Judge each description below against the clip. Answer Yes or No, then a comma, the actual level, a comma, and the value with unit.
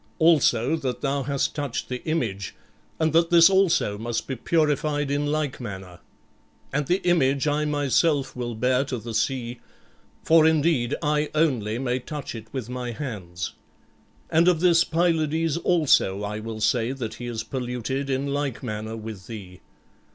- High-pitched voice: No, low, 135 Hz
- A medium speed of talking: Yes, average, 160 wpm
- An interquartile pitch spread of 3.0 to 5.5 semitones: Yes, average, 4.9 semitones